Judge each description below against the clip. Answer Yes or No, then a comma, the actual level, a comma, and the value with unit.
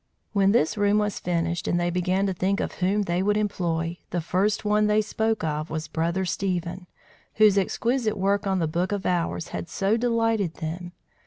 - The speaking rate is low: No, average, 190 wpm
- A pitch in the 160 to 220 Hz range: Yes, high, 190 Hz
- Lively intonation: No, average, 3.2 semitones